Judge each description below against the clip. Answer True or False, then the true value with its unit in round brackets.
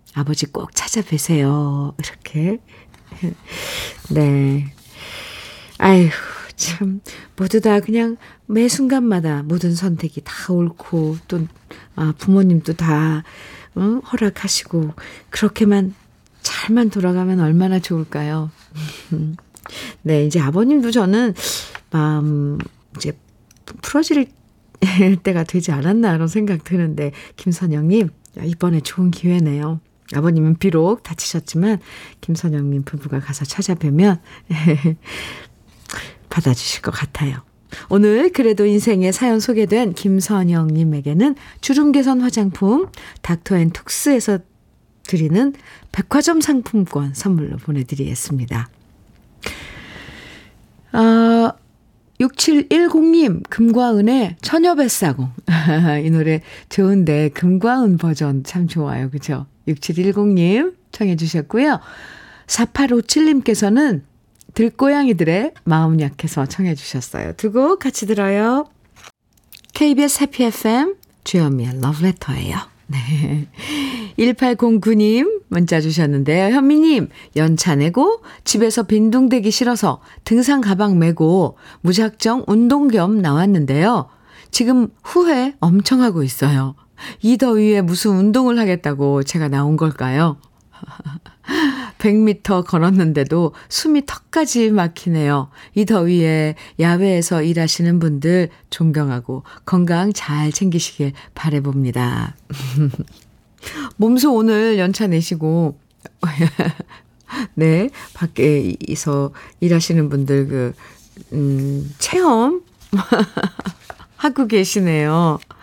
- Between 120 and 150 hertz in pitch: False (180 Hz)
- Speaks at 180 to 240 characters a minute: True (220 characters per minute)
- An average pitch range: False (6.5 semitones)